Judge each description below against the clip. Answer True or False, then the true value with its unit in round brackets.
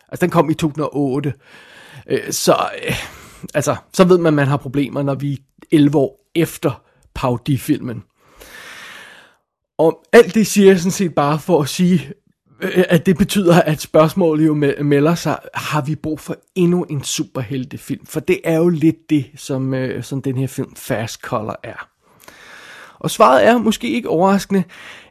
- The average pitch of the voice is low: False (155 Hz)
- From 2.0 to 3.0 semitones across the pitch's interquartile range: False (4.3 semitones)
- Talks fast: False (165 wpm)